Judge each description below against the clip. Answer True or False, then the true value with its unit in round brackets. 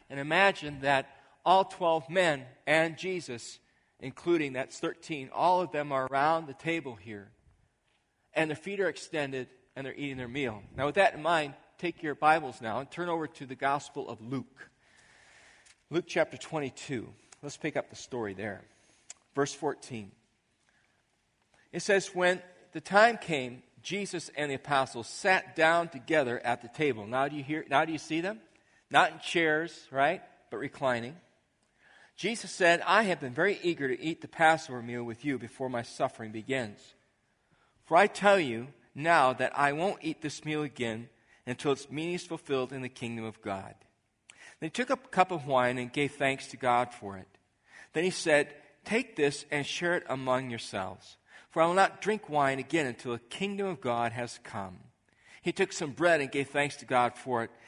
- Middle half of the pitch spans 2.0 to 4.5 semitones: False (4.9 semitones)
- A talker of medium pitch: True (145 Hz)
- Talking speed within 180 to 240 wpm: True (185 wpm)